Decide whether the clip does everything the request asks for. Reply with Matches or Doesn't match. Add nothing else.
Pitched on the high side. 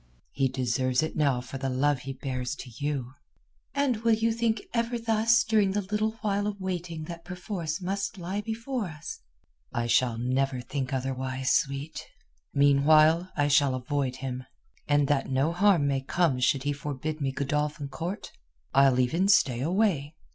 Doesn't match